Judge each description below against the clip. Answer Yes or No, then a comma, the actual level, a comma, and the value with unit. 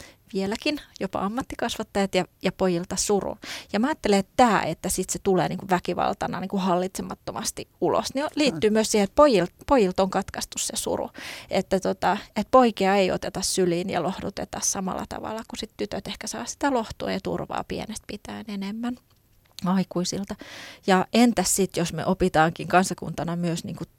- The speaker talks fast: Yes, fast, 165 wpm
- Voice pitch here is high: Yes, high, 195 Hz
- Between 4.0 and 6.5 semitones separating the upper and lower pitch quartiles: No, average, 3.5 semitones